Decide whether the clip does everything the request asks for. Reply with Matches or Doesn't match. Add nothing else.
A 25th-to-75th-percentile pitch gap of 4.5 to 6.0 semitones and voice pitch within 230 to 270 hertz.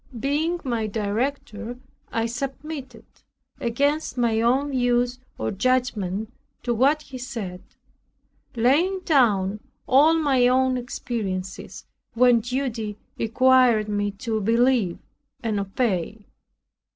Doesn't match